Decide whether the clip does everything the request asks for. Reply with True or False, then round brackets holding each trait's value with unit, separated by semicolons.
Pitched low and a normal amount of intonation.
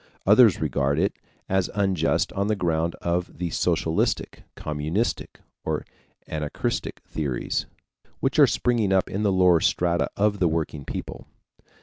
True (90 Hz; 3.8 semitones)